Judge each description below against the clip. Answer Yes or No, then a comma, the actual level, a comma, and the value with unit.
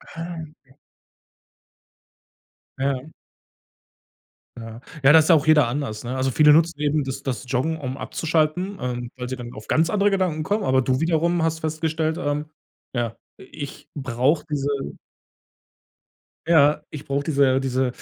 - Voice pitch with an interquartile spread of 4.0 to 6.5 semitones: No, average, 3.5 semitones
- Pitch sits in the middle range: Yes, medium, 145 Hz